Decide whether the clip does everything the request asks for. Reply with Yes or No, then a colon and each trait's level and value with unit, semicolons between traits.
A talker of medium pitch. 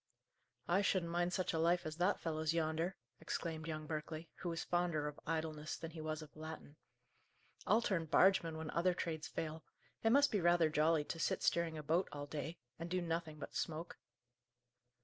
Yes: medium, 165 Hz